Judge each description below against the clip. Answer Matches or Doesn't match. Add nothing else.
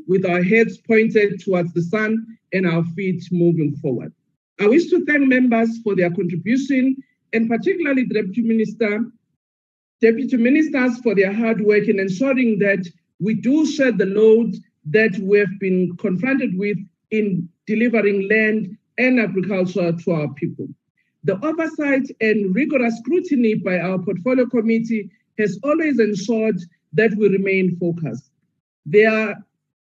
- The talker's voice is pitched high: Matches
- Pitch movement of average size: Matches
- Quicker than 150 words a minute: Doesn't match